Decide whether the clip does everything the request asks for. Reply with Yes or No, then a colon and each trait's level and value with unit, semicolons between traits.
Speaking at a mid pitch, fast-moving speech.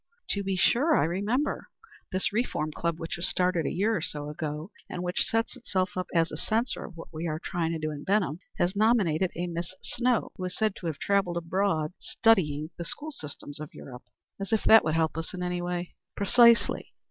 Yes: medium, 180 Hz; fast, 215 wpm